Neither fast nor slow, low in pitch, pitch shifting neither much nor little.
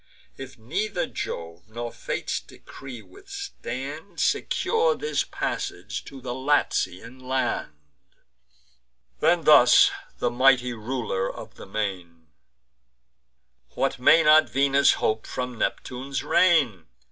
No: slow, 105 wpm; low, 130 Hz; average, 4.7 semitones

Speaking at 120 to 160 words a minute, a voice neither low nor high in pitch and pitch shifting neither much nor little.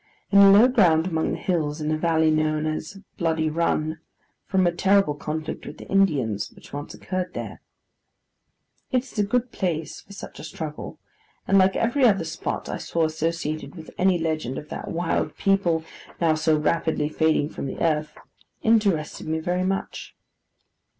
No: average, 170 wpm; medium, 165 Hz; average, 3.5 semitones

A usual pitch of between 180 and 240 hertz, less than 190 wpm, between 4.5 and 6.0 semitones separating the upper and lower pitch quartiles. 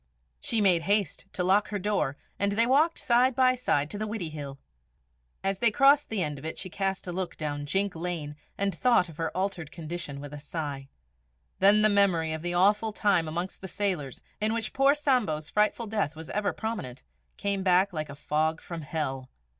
No: medium, 185 Hz; average, 200 wpm; average, 5.1 semitones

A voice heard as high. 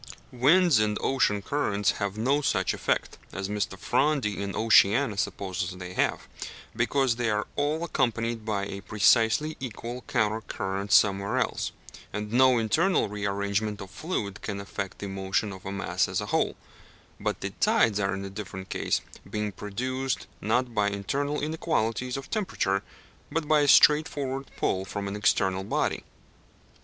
No: low, 105 Hz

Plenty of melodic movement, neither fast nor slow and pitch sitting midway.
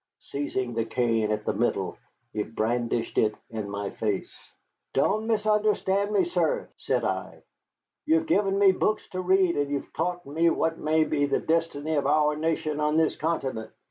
Yes: wide, 7.6 semitones; average, 175 wpm; medium, 155 Hz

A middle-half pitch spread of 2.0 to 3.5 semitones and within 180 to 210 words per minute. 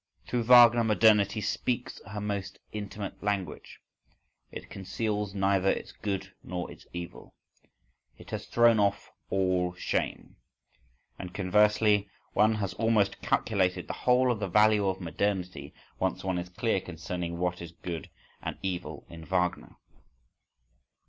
No: average, 2.8 semitones; slow, 135 wpm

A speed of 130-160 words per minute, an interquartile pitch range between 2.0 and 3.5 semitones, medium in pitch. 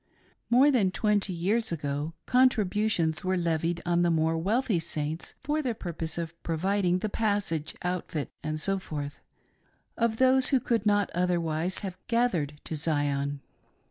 No: average, 140 wpm; average, 4.9 semitones; medium, 180 Hz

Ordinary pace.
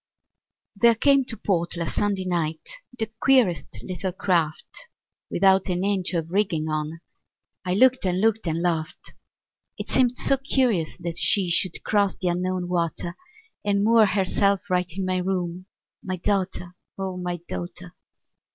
Yes: average, 150 wpm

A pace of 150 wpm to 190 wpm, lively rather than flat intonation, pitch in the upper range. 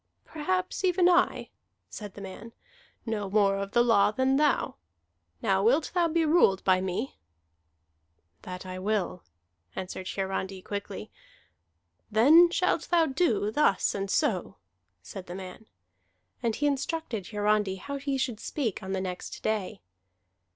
No: average, 140 wpm; wide, 6.7 semitones; high, 210 Hz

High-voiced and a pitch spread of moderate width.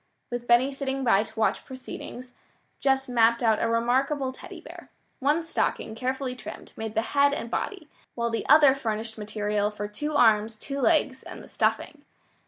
Yes: high, 245 Hz; average, 3.5 semitones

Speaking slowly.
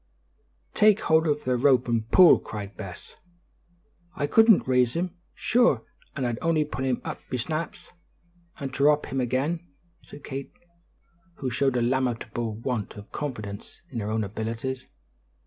No: average, 150 wpm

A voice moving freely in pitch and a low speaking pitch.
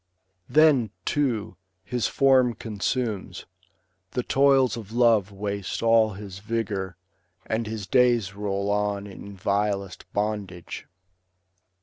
No: average, 3.2 semitones; low, 105 Hz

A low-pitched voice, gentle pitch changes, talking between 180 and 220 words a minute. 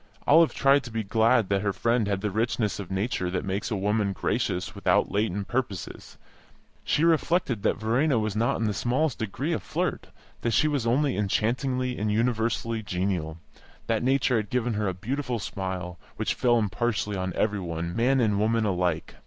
No: low, 110 Hz; average, 3.9 semitones; average, 185 wpm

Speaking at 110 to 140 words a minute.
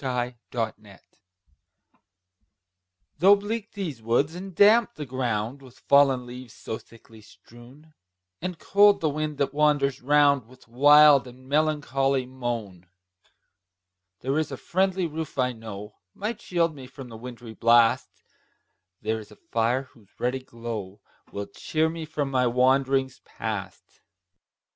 Yes: slow, 135 wpm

